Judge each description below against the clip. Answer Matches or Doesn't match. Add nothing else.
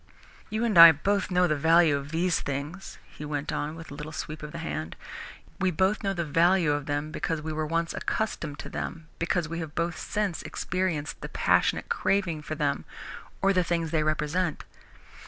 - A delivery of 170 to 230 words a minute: Matches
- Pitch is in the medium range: Matches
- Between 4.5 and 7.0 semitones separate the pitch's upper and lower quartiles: Doesn't match